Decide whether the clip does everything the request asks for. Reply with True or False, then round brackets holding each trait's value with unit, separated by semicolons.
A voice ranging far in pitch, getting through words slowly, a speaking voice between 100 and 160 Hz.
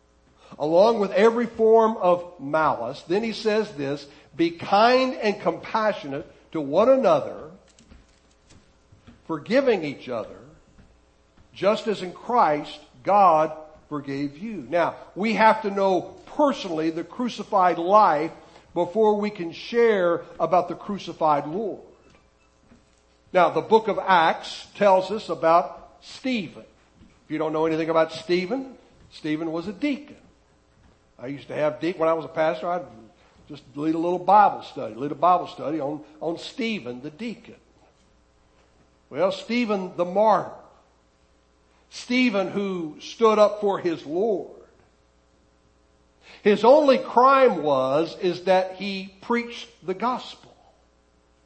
False (6.5 semitones; 130 wpm; 170 Hz)